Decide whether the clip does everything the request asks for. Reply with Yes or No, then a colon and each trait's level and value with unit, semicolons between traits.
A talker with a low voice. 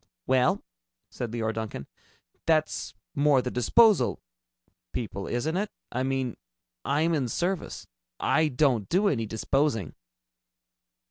Yes: low, 130 Hz